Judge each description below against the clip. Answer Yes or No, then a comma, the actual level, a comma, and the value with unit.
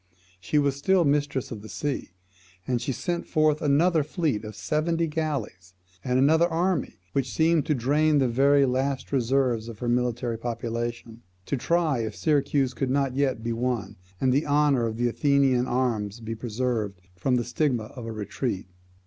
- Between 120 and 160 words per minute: No, average, 175 wpm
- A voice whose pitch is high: No, low, 130 Hz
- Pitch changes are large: No, average, 4.0 semitones